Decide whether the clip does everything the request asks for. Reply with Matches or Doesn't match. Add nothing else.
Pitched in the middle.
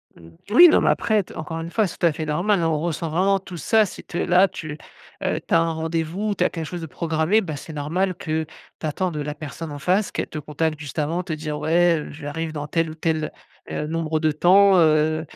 Matches